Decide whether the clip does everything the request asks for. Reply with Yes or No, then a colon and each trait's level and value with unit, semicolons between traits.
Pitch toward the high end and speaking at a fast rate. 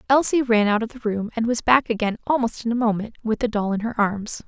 Yes: high, 225 Hz; fast, 270 wpm